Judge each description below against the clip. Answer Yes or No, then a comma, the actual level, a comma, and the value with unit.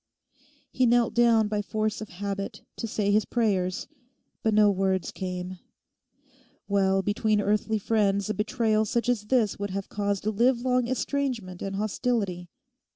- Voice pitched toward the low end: No, high, 210 Hz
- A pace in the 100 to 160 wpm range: Yes, average, 150 wpm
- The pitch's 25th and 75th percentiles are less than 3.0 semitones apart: Yes, narrow, 2.6 semitones